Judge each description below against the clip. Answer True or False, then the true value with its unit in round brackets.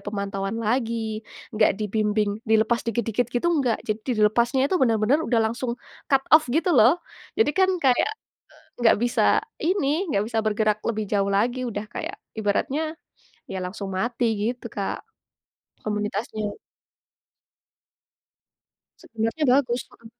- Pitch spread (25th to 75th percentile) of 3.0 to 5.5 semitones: True (3.4 semitones)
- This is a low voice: False (230 Hz)